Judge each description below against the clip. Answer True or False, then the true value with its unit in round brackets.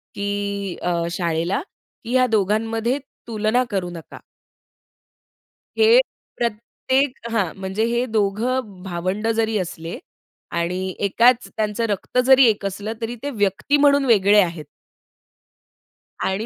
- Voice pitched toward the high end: True (210 Hz)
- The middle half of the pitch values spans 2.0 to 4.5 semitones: True (3.8 semitones)